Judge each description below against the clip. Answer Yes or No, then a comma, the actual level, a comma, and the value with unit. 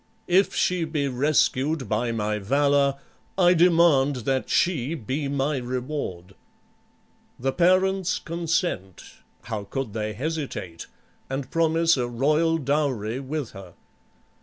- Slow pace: Yes, slow, 115 wpm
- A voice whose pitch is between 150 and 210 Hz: No, medium, 140 Hz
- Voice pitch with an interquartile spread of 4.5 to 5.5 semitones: Yes, average, 5.2 semitones